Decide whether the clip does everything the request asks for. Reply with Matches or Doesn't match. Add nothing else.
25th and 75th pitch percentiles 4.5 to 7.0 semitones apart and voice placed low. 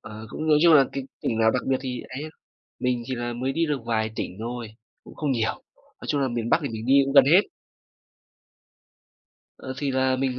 Doesn't match